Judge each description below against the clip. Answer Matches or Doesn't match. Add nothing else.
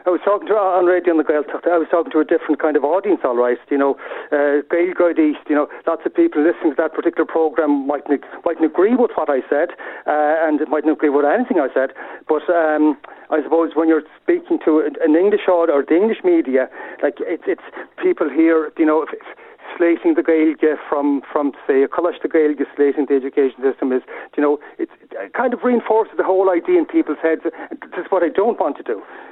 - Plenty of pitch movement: Doesn't match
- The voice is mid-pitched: Matches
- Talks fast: Matches